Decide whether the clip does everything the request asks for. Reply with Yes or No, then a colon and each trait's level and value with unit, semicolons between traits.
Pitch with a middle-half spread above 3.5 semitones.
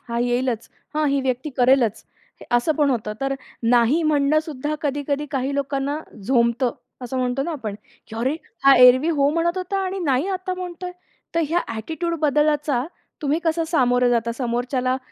Yes: average, 3.9 semitones